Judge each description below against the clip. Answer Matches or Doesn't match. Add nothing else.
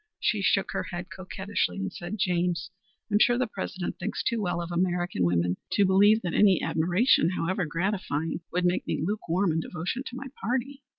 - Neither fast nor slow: Matches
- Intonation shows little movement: Doesn't match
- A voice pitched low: Doesn't match